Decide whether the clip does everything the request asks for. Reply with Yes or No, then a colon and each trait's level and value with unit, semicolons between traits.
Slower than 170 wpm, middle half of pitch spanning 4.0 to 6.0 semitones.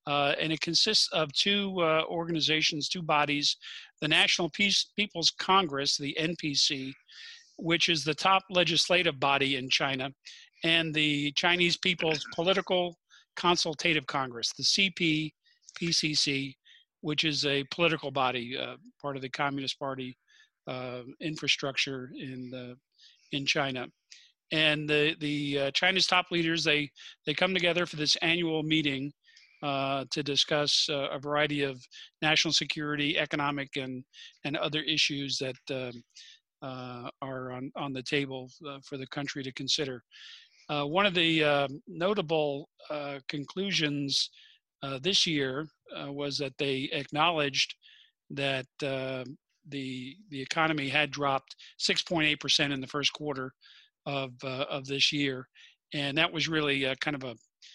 No: average, 145 wpm; average, 3.3 semitones